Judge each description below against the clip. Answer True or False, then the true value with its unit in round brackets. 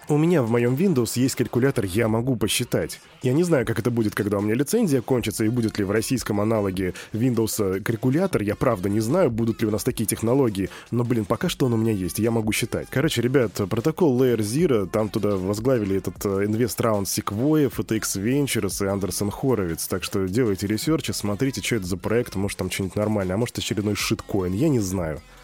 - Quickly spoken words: True (205 wpm)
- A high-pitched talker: False (115 Hz)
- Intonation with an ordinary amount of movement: True (3.7 semitones)